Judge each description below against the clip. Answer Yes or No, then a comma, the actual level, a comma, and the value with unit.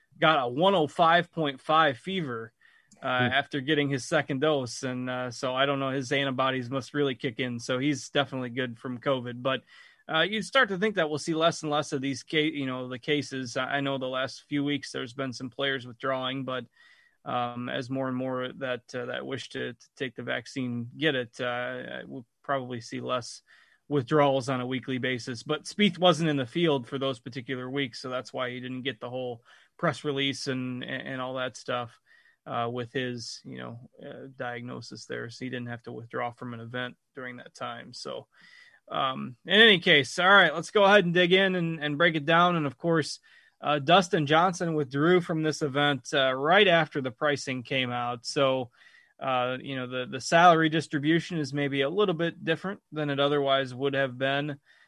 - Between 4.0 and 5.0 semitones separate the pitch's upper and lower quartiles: No, average, 3.4 semitones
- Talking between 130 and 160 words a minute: No, average, 200 wpm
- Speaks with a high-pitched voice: No, low, 135 Hz